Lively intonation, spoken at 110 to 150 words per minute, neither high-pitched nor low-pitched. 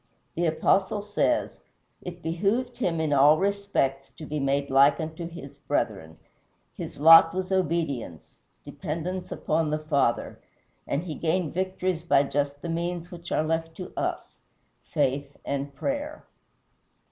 No: average, 4.2 semitones; average, 140 wpm; medium, 165 Hz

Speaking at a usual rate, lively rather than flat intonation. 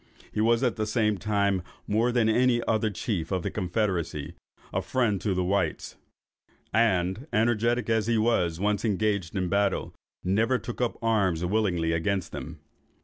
No: average, 170 wpm; average, 3.7 semitones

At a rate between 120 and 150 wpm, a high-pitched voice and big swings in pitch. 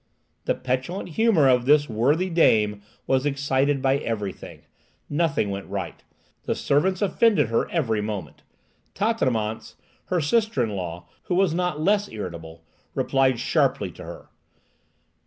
No: slow, 135 wpm; low, 135 Hz; wide, 7.9 semitones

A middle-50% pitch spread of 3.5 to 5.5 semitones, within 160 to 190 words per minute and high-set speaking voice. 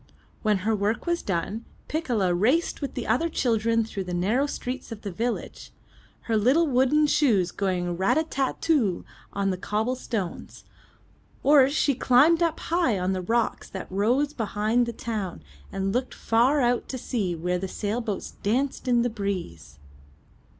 Yes: average, 5.1 semitones; average, 165 wpm; high, 225 Hz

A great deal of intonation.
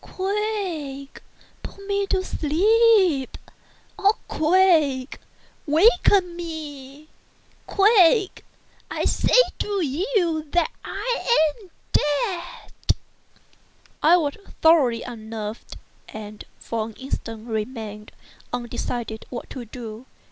Yes: wide, 7.6 semitones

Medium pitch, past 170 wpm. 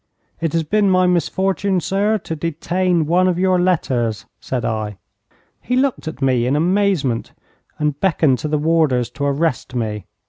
No: medium, 160 Hz; average, 165 wpm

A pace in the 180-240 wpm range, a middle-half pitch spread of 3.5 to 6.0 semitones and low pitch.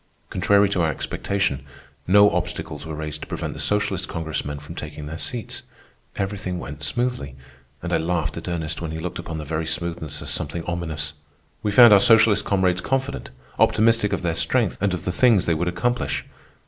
Yes: average, 185 wpm; average, 4.3 semitones; very low, 85 Hz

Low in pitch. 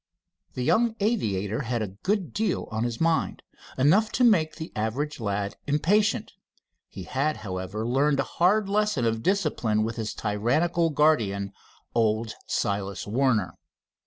Yes: low, 125 Hz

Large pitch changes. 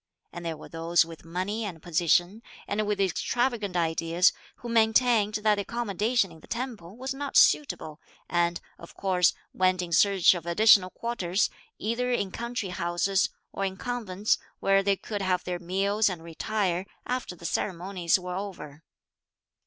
No: average, 3.8 semitones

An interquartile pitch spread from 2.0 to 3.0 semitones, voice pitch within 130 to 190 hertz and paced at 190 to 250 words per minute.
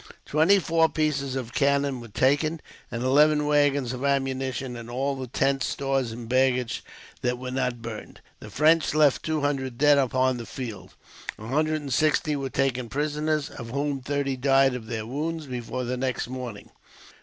No: average, 2.7 semitones; low, 135 Hz; average, 175 wpm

